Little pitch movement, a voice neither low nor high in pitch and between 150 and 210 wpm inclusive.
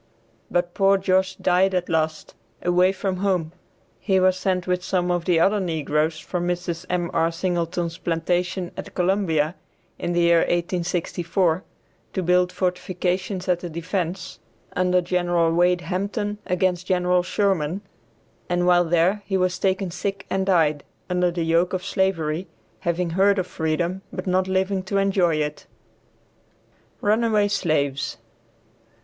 No: narrow, 1.8 semitones; medium, 180 Hz; average, 140 wpm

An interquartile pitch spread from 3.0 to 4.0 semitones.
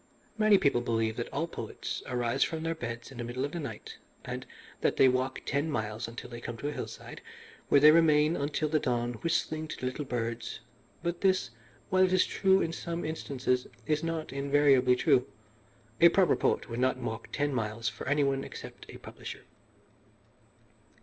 No: average, 4.7 semitones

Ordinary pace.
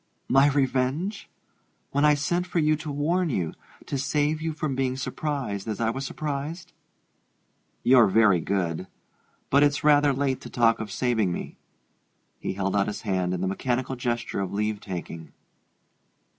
Yes: average, 160 wpm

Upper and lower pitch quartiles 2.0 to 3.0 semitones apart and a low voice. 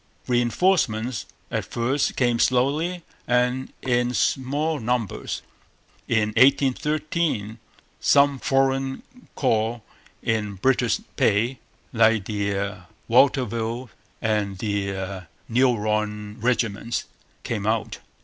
No: average, 3.7 semitones; low, 120 Hz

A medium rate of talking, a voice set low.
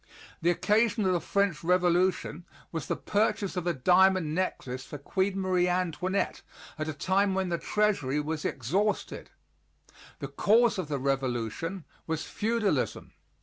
No: average, 145 wpm; medium, 180 Hz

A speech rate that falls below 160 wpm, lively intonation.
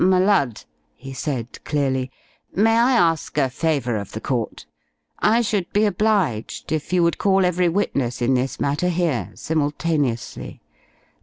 Yes: average, 150 wpm; wide, 6.1 semitones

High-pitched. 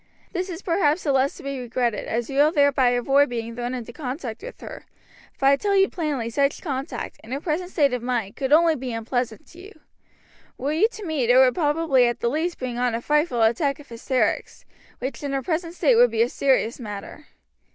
Yes: very high, 270 Hz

